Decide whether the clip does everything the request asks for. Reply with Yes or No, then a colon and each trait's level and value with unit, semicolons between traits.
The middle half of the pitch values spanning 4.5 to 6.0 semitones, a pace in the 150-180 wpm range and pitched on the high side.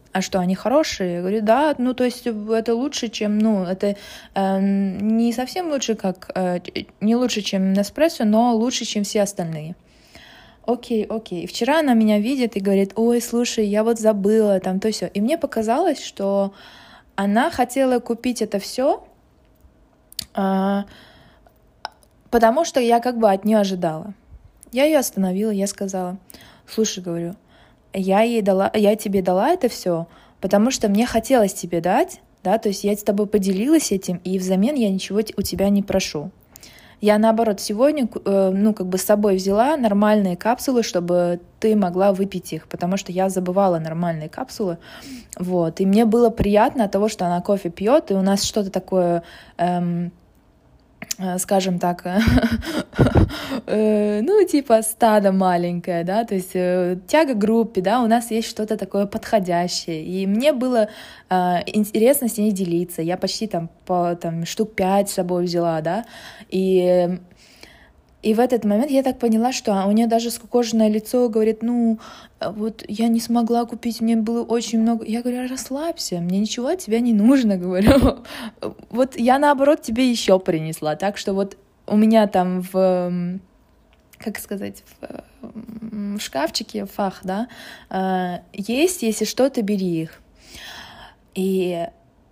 No: average, 3.7 semitones; average, 155 wpm; high, 210 Hz